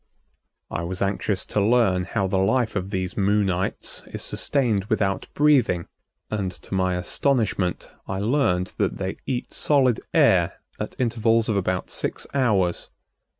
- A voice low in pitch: Yes, low, 100 Hz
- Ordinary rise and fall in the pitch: Yes, average, 4.1 semitones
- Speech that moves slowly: No, average, 145 wpm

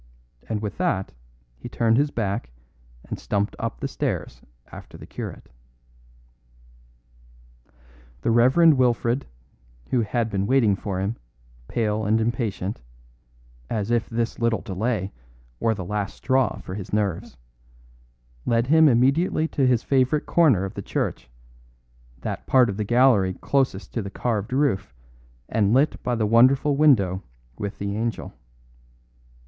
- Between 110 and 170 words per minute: Yes, average, 140 wpm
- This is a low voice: Yes, low, 115 Hz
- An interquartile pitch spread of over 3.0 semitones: Yes, average, 4.3 semitones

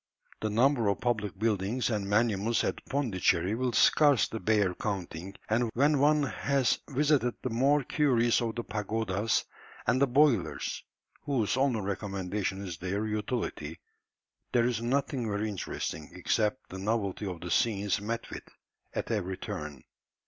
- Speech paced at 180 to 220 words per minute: No, average, 145 wpm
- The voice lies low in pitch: Yes, low, 110 Hz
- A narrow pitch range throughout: No, average, 4.0 semitones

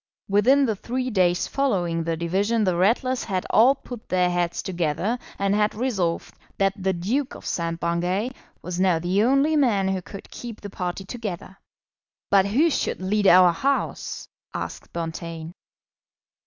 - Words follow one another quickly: No, average, 155 wpm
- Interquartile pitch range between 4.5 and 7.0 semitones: Yes, average, 4.8 semitones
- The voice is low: No, high, 195 Hz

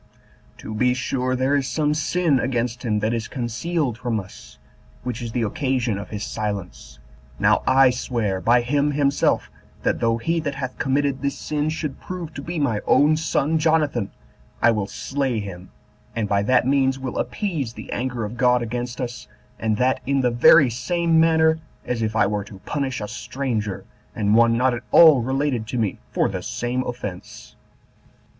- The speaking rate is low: No, average, 180 wpm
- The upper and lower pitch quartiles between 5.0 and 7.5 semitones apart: No, average, 4.0 semitones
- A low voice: Yes, low, 125 Hz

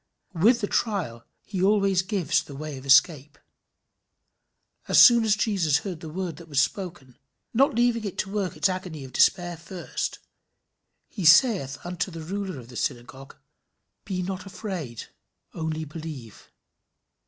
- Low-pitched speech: No, medium, 175 Hz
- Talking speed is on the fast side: No, average, 150 wpm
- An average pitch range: Yes, average, 4.8 semitones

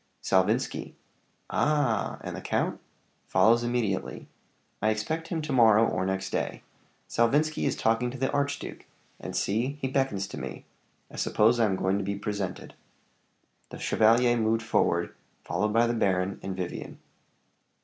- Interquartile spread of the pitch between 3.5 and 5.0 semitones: Yes, average, 4.2 semitones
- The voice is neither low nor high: No, low, 115 Hz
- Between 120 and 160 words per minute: Yes, average, 150 wpm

